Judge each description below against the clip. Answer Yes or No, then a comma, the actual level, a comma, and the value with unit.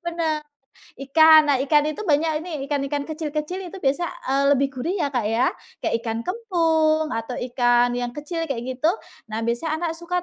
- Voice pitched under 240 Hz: No, very high, 300 Hz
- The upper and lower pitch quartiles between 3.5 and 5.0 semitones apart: Yes, average, 4.2 semitones